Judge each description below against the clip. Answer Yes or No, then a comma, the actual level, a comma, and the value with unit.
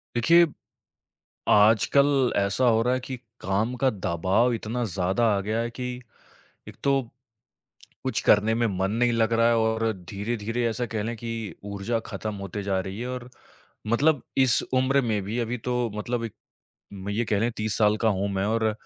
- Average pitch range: Yes, average, 3.0 semitones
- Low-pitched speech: Yes, low, 115 Hz